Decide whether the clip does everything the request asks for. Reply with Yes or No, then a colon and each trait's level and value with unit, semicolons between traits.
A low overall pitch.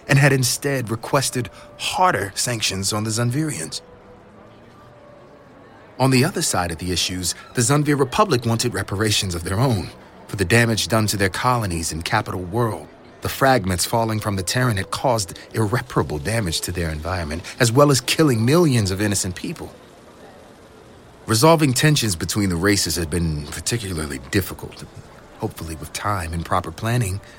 Yes: low, 110 Hz